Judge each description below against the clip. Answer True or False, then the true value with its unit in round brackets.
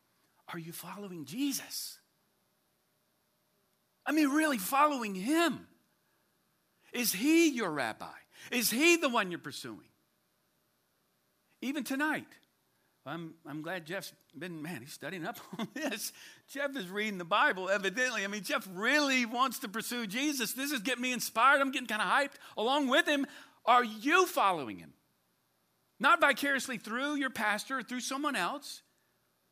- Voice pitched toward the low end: False (250 Hz)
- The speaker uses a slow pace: False (145 wpm)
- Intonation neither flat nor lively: False (5.7 semitones)